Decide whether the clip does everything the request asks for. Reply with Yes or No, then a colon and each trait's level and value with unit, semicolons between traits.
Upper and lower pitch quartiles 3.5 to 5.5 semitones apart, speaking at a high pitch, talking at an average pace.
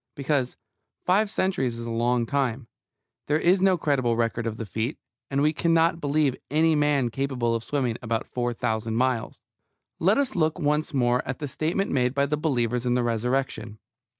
No: average, 4.4 semitones; low, 135 Hz; average, 180 wpm